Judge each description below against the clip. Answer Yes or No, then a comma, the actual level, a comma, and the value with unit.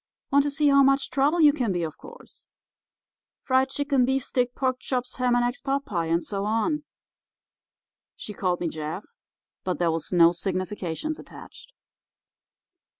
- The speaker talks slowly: Yes, slow, 110 wpm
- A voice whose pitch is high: Yes, high, 245 Hz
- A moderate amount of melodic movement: No, wide, 7.4 semitones